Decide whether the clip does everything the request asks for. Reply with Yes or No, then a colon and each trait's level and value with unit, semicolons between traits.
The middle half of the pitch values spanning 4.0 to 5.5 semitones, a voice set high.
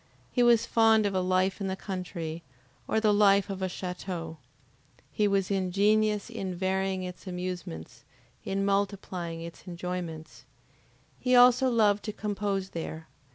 No: narrow, 2.6 semitones; high, 195 Hz